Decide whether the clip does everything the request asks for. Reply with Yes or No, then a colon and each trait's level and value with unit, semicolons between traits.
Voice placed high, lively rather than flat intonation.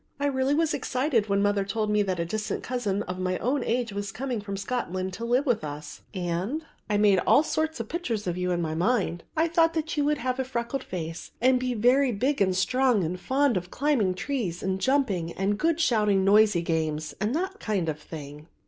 Yes: high, 215 Hz; wide, 6.1 semitones